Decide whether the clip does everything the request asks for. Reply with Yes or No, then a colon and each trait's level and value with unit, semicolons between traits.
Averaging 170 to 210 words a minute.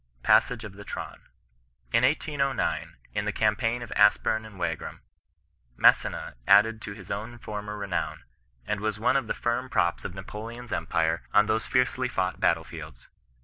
No: average, 155 wpm